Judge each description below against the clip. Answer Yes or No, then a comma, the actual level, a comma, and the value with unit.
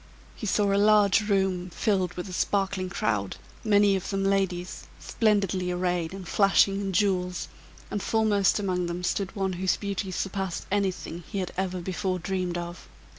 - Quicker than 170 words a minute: No, average, 165 wpm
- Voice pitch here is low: No, high, 190 Hz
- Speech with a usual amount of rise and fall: No, narrow, 1.8 semitones